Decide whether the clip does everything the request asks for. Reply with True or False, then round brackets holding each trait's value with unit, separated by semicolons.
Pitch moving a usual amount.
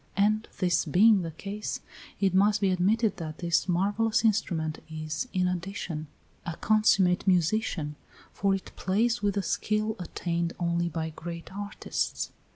True (3.5 semitones)